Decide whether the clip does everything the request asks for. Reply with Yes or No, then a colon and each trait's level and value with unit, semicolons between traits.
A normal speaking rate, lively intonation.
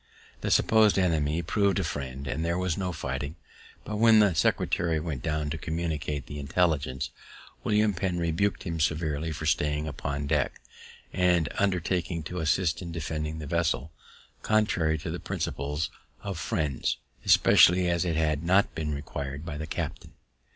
No: average, 160 wpm; average, 3.2 semitones